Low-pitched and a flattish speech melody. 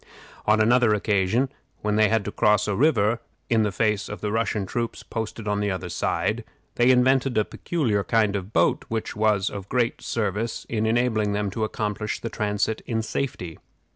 Yes: low, 110 Hz; narrow, 1.9 semitones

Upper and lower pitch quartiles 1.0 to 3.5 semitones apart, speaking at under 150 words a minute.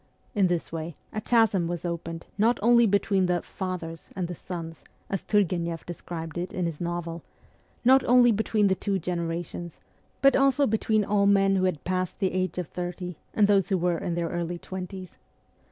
No: average, 2.9 semitones; average, 195 wpm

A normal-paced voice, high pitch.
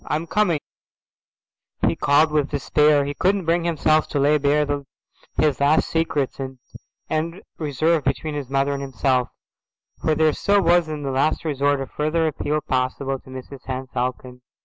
No: average, 165 wpm; medium, 145 Hz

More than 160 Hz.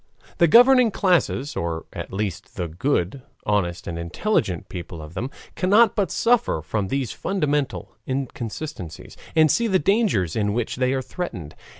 No: low, 130 Hz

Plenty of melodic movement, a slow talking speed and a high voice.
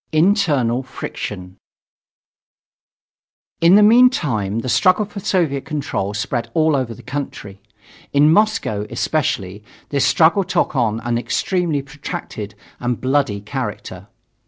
No: wide, 6.7 semitones; slow, 115 wpm; low, 135 Hz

